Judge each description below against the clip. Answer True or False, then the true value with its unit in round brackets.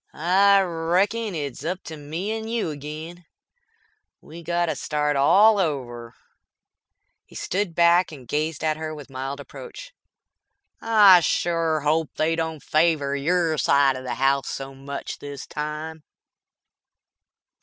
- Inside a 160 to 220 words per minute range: False (135 wpm)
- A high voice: False (160 Hz)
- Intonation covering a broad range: False (3.5 semitones)